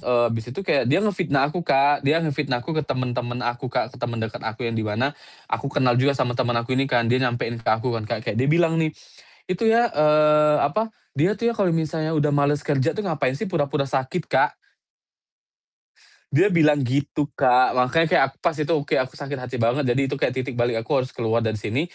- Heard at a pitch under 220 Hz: Yes, medium, 140 Hz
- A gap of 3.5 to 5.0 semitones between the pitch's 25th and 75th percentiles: Yes, average, 4.0 semitones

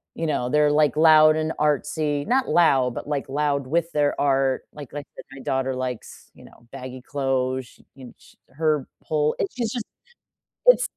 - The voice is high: No, medium, 145 Hz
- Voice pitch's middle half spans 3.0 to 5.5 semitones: No, narrow, 2.6 semitones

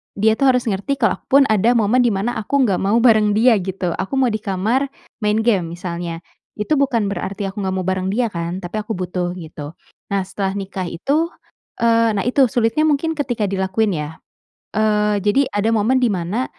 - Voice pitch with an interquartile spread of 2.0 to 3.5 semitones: No, average, 4.2 semitones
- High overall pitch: Yes, high, 210 Hz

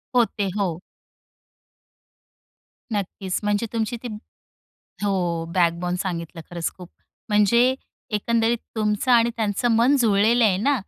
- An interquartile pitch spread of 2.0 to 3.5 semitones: No, average, 4.2 semitones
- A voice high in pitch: Yes, high, 210 Hz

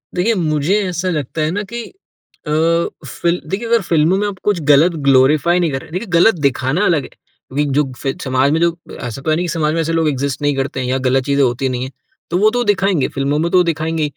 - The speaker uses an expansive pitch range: No, average, 4.5 semitones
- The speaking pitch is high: No, medium, 155 Hz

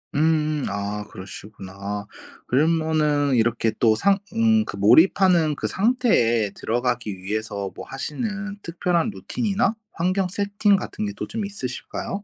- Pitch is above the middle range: No, medium, 155 Hz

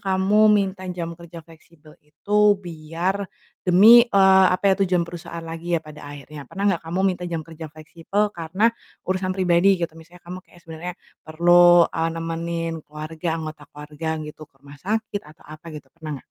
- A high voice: No, medium, 170 Hz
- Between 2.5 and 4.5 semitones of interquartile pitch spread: Yes, average, 2.8 semitones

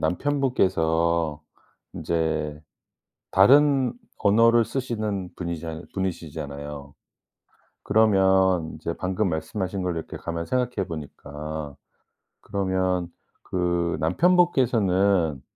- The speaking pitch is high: No, very low, 90 Hz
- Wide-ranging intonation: No, average, 4.7 semitones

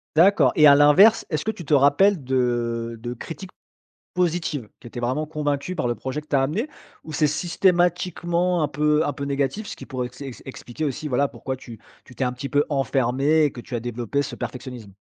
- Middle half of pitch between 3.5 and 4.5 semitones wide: Yes, average, 4.0 semitones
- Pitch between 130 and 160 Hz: Yes, medium, 140 Hz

